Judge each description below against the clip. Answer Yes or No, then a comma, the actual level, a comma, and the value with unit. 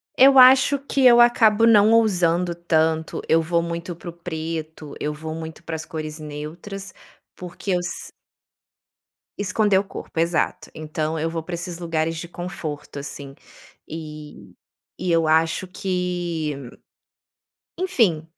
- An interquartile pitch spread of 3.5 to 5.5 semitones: No, average, 3.0 semitones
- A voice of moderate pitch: Yes, medium, 170 Hz